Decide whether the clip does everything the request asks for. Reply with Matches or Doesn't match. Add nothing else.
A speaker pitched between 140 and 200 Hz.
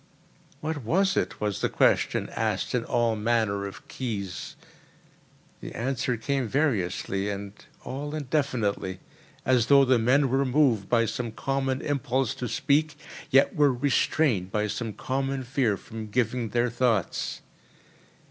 Doesn't match